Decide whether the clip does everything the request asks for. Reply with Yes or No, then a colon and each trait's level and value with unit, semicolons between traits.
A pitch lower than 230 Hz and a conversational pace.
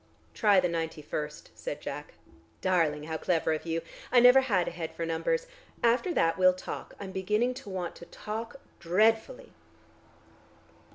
Yes: medium, 185 Hz; average, 160 wpm